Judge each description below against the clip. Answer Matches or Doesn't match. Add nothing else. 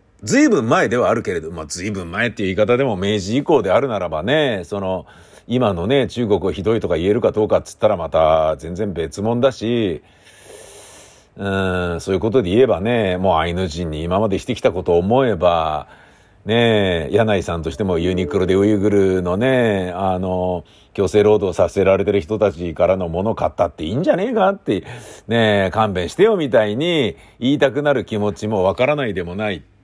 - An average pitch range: Matches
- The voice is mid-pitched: Doesn't match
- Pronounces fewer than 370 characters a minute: Doesn't match